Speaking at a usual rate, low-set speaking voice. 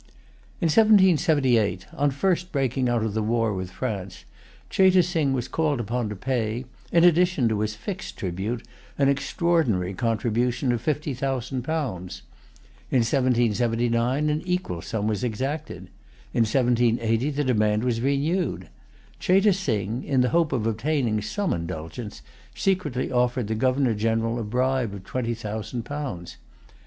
Yes: average, 145 wpm; low, 125 Hz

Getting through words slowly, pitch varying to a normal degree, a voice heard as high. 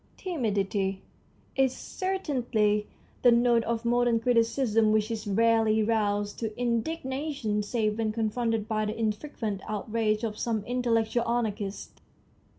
No: slow, 125 wpm; narrow, 2.2 semitones; high, 225 Hz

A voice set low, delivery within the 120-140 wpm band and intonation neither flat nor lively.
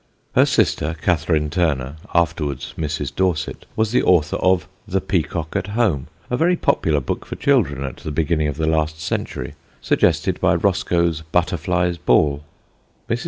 No: very low, 80 Hz; average, 155 wpm; average, 3.0 semitones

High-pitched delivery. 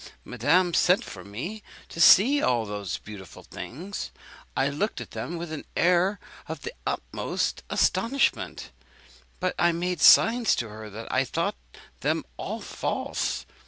No: medium, 170 Hz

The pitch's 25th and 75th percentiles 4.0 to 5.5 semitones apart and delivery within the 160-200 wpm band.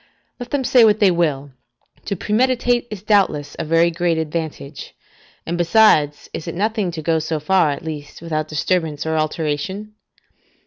Yes: average, 5.1 semitones; average, 165 wpm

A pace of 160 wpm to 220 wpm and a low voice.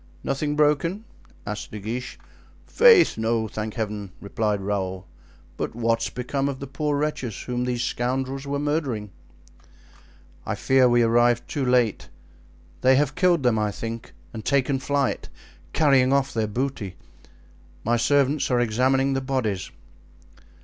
No: average, 140 wpm; low, 125 Hz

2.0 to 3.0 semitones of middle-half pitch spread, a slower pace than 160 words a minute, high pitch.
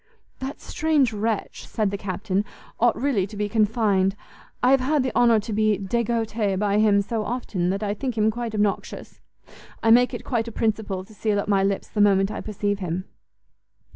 No: narrow, 2.6 semitones; average, 195 wpm; high, 215 Hz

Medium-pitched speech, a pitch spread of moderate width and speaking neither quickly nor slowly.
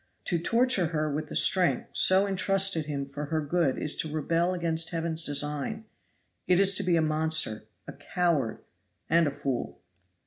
Yes: medium, 165 Hz; average, 3.4 semitones; average, 170 wpm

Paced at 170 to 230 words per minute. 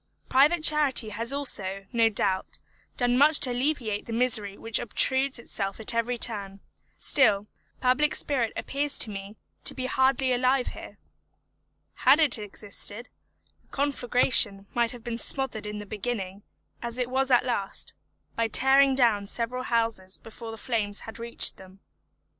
No: average, 155 wpm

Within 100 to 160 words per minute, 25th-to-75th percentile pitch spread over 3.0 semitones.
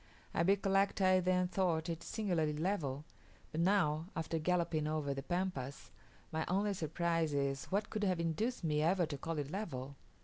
No: average, 170 wpm; average, 3.7 semitones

